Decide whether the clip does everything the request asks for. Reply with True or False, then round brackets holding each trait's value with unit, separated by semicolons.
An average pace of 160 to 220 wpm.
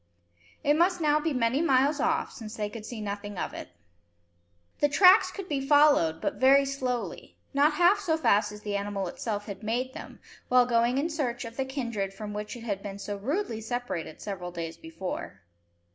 True (190 wpm)